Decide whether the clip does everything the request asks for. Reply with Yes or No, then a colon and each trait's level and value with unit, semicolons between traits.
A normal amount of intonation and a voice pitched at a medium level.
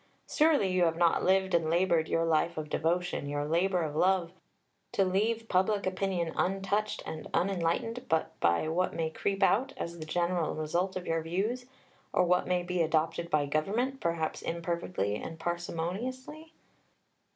Yes: average, 3.0 semitones; medium, 175 Hz